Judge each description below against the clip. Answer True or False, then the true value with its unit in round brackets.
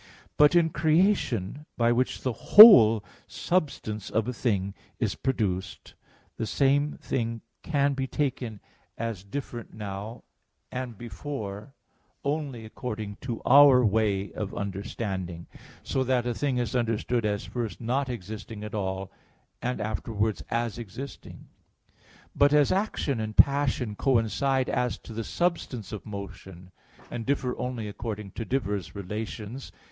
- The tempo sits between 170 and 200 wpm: False (135 wpm)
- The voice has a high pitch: False (115 Hz)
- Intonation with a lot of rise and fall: False (4.2 semitones)